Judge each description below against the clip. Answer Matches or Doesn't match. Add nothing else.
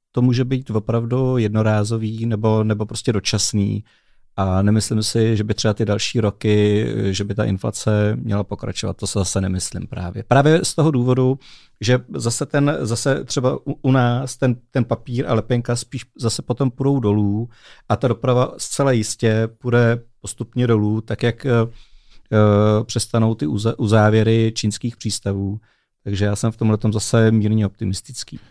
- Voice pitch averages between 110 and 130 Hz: Matches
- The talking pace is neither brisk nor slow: Matches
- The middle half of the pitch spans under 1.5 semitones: Doesn't match